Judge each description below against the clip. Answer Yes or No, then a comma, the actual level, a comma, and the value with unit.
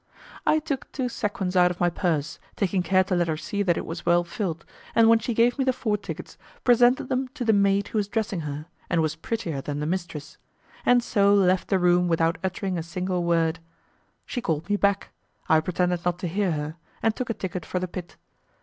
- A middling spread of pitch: Yes, average, 3.7 semitones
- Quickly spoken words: Yes, fast, 220 wpm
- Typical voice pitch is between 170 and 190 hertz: Yes, medium, 185 Hz